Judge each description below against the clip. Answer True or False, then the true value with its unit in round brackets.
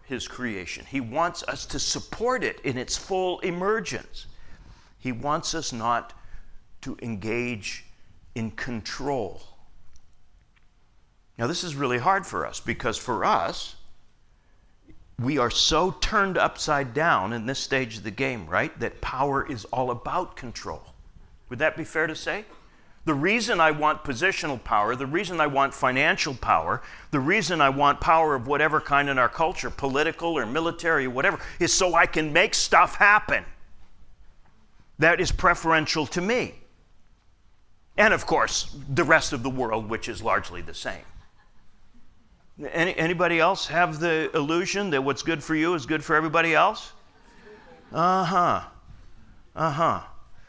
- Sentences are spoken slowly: False (150 wpm)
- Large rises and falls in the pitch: True (6.7 semitones)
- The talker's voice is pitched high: False (140 Hz)